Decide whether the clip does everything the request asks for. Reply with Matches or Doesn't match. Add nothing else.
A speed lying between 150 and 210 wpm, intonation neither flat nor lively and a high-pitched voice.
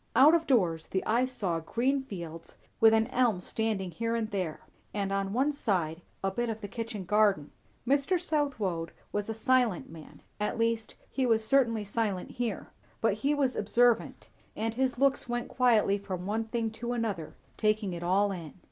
Matches